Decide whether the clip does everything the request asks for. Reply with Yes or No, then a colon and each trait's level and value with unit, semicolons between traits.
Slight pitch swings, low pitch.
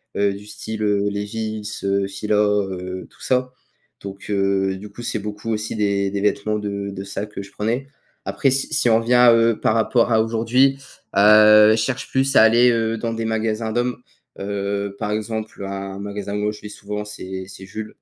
Yes: narrow, 2.0 semitones; low, 105 Hz